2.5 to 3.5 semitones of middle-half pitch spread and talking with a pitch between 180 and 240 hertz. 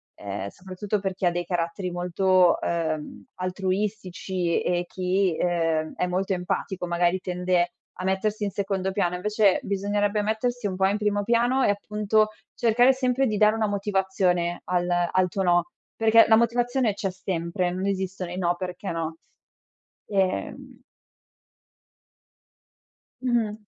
Yes: average, 2.9 semitones; high, 190 Hz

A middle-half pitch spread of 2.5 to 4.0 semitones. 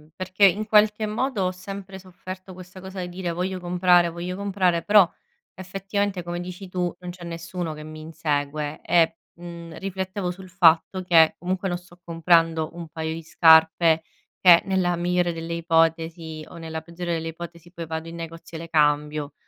No: narrow, 2.1 semitones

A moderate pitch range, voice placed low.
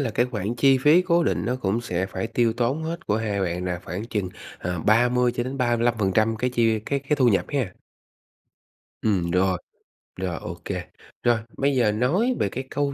Yes: average, 4.5 semitones; low, 120 Hz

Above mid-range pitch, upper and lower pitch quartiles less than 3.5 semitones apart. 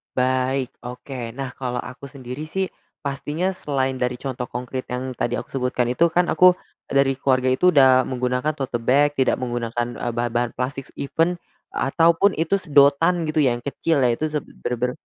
No: low, 130 Hz; average, 2.9 semitones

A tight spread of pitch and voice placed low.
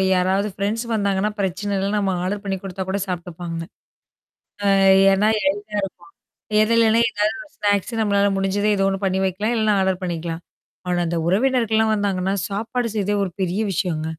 No: narrow, 2.2 semitones; high, 200 Hz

